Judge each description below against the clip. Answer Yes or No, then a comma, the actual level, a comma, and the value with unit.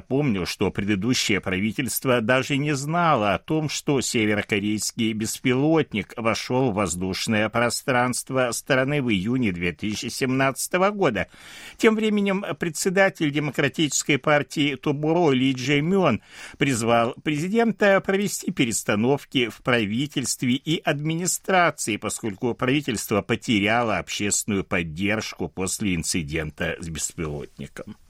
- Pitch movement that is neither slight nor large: No, wide, 6.5 semitones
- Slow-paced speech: Yes, slow, 100 wpm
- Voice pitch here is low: Yes, low, 130 Hz